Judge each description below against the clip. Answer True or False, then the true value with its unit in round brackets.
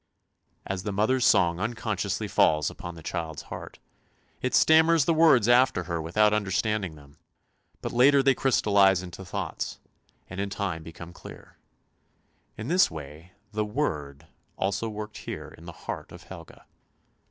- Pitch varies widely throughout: True (5.8 semitones)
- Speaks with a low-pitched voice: True (100 Hz)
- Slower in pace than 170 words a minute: True (155 wpm)